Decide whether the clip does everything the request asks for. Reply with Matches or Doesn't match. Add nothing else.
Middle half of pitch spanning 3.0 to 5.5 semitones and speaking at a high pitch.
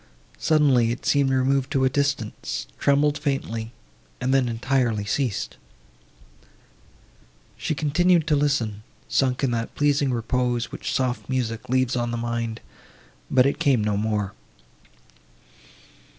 Doesn't match